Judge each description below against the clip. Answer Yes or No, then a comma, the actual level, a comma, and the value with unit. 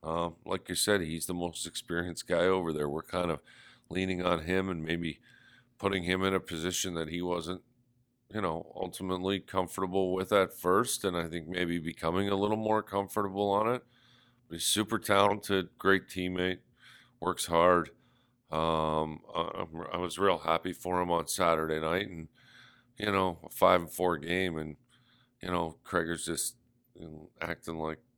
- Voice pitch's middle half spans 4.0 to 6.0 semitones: No, average, 2.9 semitones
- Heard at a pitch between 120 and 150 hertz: No, very low, 90 Hz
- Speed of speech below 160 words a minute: No, average, 175 wpm